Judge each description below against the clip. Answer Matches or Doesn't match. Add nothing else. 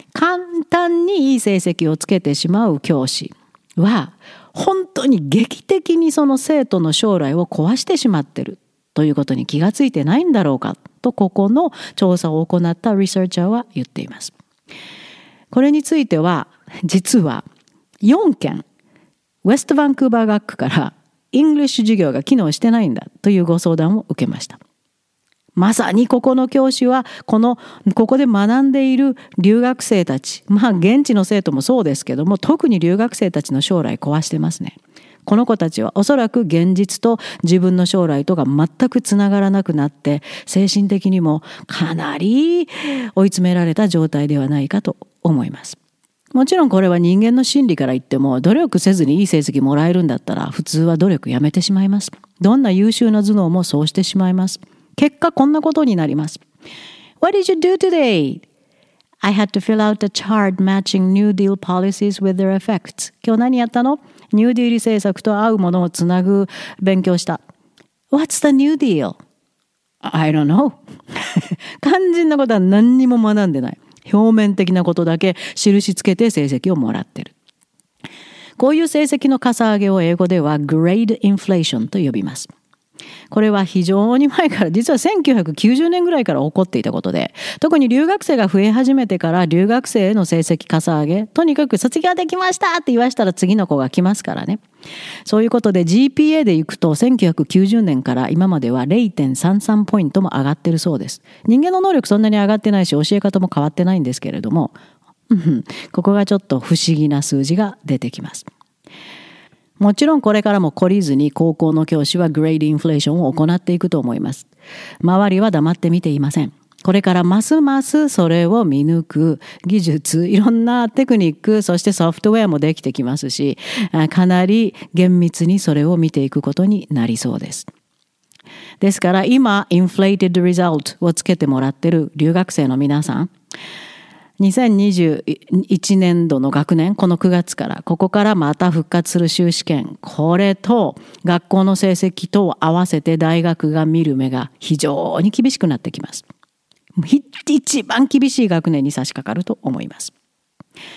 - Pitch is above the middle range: Matches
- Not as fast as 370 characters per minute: Matches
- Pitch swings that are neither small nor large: Doesn't match